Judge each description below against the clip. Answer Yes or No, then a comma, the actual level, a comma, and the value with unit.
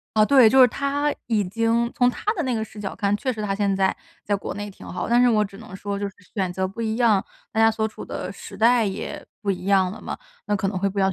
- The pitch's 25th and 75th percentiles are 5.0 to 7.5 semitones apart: No, average, 2.9 semitones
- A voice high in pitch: Yes, high, 210 Hz